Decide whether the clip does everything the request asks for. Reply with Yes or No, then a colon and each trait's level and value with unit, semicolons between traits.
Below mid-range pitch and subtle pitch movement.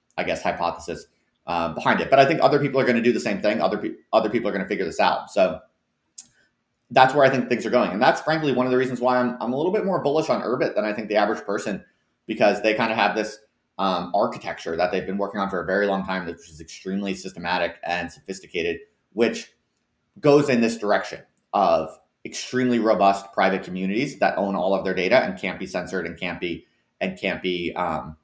No: low, 110 Hz; average, 5.2 semitones